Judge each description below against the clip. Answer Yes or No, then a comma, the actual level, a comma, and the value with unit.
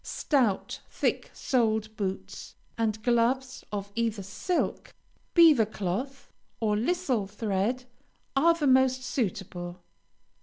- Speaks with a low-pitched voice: No, high, 230 Hz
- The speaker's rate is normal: No, slow, 105 wpm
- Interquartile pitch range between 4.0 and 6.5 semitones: Yes, average, 4.4 semitones